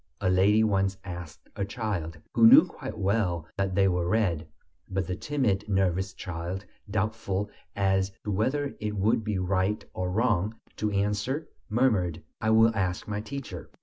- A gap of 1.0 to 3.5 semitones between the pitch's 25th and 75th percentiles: Yes, average, 2.8 semitones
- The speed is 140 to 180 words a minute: Yes, average, 160 wpm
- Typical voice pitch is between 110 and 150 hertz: No, low, 100 Hz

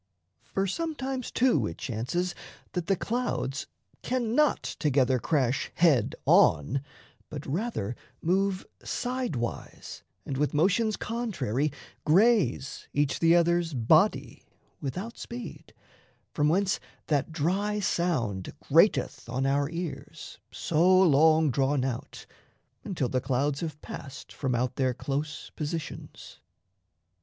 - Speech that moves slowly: Yes, slow, 115 wpm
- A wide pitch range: Yes, wide, 6.3 semitones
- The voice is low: No, medium, 155 Hz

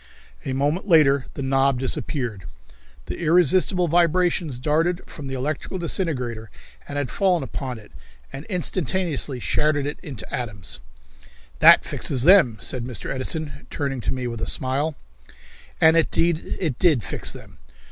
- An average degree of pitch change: Yes, average, 4.6 semitones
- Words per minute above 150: No, average, 145 wpm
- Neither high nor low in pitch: Yes, medium, 145 Hz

